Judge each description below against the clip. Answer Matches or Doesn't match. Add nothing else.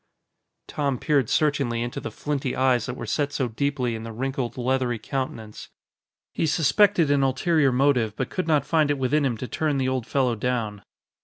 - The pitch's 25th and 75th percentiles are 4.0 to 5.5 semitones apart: Doesn't match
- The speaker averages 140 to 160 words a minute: Doesn't match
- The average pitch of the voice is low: Matches